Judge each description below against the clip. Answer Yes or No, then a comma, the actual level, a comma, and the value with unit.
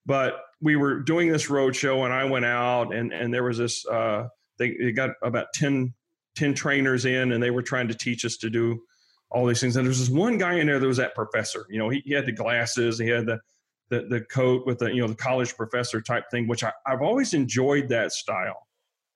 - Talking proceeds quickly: Yes, fast, 245 wpm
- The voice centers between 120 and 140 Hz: Yes, low, 125 Hz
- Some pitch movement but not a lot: No, narrow, 2.1 semitones